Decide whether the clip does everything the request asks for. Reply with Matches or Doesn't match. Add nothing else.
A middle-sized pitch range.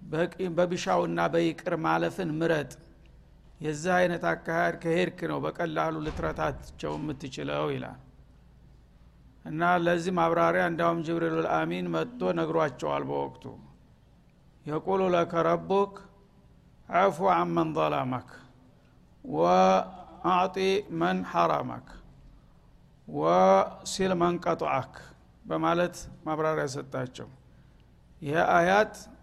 Matches